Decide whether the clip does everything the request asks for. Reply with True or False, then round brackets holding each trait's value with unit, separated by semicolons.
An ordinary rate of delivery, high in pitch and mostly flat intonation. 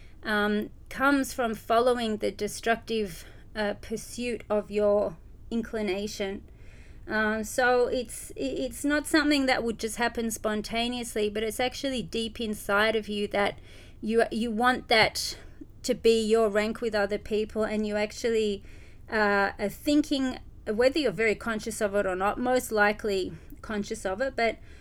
True (150 wpm; 220 Hz; 2.3 semitones)